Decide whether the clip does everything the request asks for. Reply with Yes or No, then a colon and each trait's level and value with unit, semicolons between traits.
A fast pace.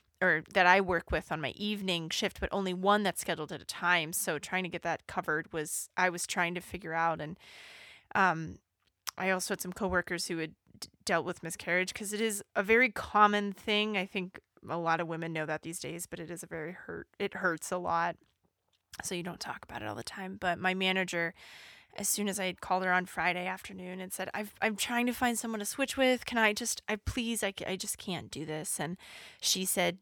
Yes: fast, 230 wpm